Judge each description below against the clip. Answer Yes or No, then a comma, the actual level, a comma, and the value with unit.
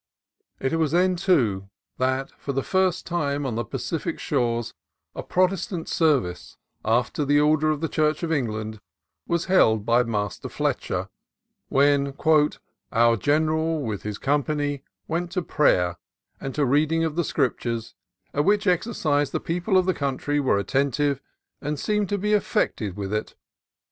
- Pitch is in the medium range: Yes, medium, 145 Hz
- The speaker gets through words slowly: No, average, 160 wpm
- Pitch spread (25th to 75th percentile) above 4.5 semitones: Yes, wide, 5.4 semitones